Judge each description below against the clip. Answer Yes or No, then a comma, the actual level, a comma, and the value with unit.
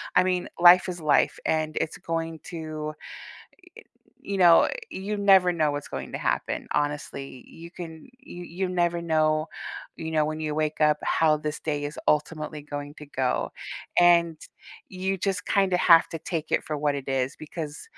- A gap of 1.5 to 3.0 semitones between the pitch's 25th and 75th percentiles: Yes, narrow, 2.6 semitones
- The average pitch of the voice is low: No, medium, 160 Hz